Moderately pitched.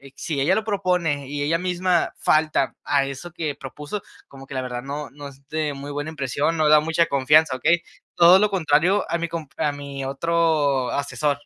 Yes: medium, 150 Hz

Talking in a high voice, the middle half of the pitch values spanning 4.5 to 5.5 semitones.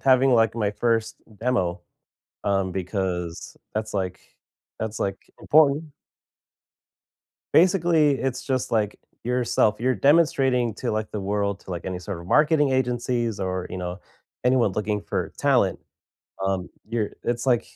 No: low, 110 Hz; average, 5.0 semitones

